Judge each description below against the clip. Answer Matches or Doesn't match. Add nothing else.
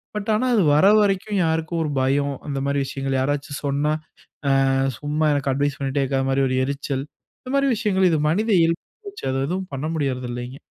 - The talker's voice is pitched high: Doesn't match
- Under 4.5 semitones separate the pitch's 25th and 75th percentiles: Doesn't match